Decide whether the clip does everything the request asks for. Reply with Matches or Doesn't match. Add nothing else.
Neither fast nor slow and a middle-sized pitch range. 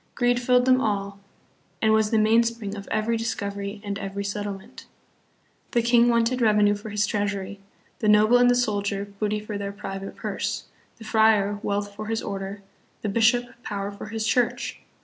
Doesn't match